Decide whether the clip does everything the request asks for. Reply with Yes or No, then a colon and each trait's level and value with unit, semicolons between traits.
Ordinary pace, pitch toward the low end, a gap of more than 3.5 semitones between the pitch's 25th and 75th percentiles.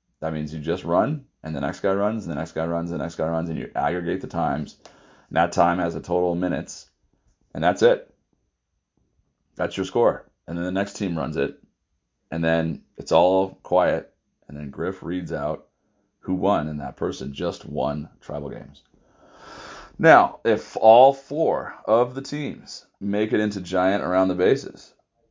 Yes: average, 185 wpm; very low, 90 Hz; average, 4.1 semitones